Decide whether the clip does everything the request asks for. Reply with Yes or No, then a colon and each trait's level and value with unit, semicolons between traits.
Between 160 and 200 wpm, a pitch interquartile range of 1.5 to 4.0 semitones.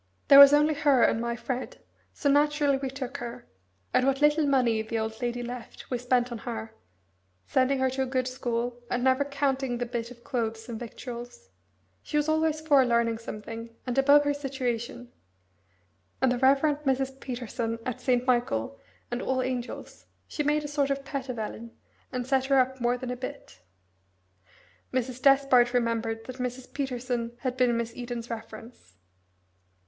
Yes: average, 175 wpm; narrow, 2.4 semitones